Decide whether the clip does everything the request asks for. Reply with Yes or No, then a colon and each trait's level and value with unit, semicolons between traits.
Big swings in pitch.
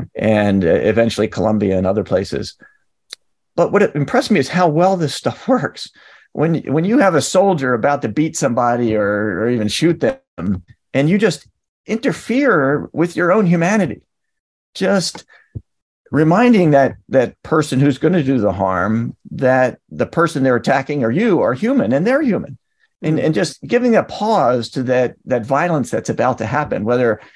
Yes: wide, 8.7 semitones